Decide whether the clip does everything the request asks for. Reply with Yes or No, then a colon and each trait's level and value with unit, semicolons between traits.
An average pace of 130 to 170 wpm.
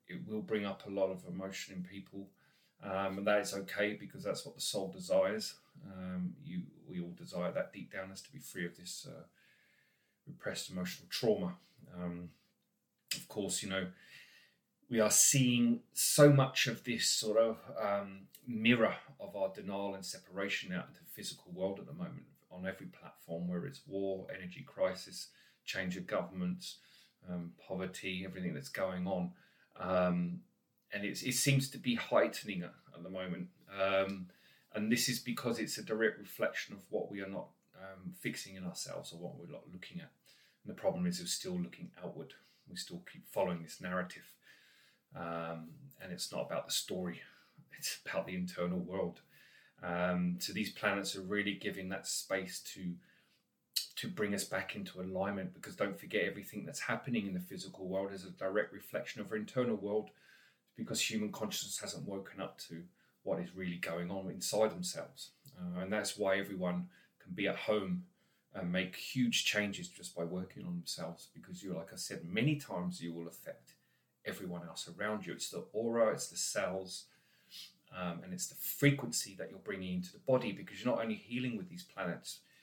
No: average, 185 wpm